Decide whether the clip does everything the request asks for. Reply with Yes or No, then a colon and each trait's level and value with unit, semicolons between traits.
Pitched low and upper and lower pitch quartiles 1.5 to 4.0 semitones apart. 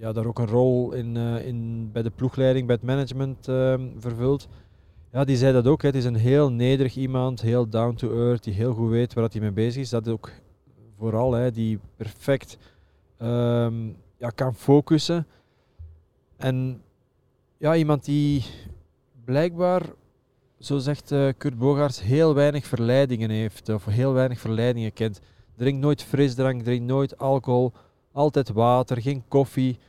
Yes: low, 125 Hz; average, 3.0 semitones